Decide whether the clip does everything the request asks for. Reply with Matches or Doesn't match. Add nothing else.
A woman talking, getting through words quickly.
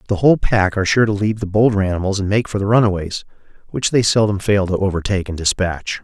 Doesn't match